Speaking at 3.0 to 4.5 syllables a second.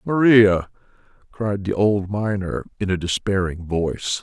Yes: 4.1 syllables/s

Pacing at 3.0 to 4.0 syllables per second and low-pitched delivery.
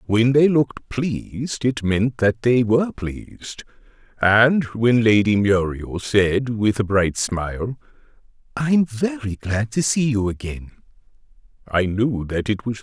Yes: 3.9 syllables/s; low, 115 Hz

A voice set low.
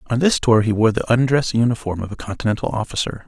Yes: low, 115 Hz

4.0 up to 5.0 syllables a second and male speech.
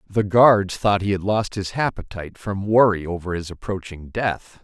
Yes: 4.7 syllables/s; male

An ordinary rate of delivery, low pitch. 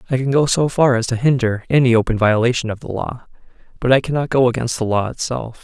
No: fast, 235 wpm; low, 125 Hz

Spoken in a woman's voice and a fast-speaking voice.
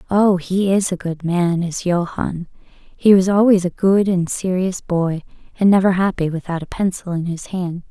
No: female; average, 190 wpm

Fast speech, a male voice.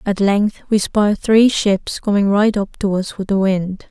No: fast, 215 wpm; female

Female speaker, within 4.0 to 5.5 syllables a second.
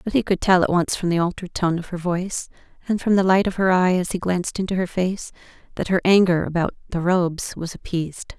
No: female; 6.1 syllables/s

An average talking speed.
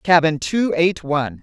Yes: average, 170 wpm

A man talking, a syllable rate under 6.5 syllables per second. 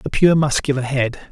Yes: male; 4.7 syllables/s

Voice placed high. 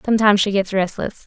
Yes: high, 200 Hz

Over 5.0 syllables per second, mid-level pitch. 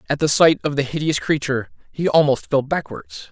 Yes: 5.5 syllables/s; medium, 145 Hz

